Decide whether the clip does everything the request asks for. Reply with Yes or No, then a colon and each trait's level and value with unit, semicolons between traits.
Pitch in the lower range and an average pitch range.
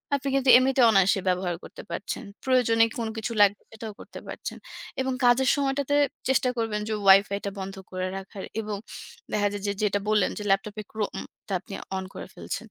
No: high, 215 Hz; average, 4.2 semitones